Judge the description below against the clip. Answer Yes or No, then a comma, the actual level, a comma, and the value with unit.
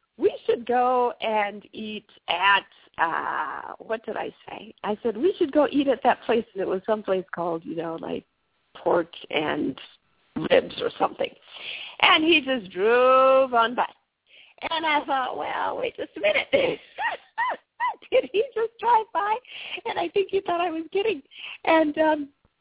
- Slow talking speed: No, average, 165 wpm